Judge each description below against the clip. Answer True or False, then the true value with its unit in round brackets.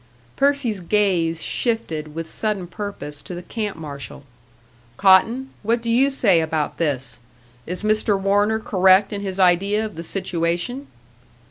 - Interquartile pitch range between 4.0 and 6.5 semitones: True (4.4 semitones)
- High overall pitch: True (195 Hz)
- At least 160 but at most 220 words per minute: False (140 wpm)